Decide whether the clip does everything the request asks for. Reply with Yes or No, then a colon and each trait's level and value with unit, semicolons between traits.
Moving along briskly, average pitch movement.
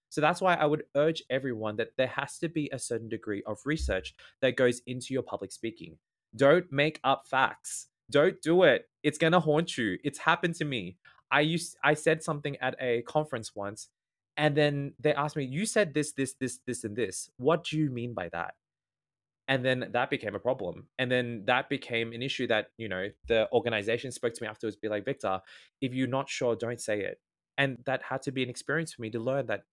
Yes: fast, 220 wpm; average, 4.3 semitones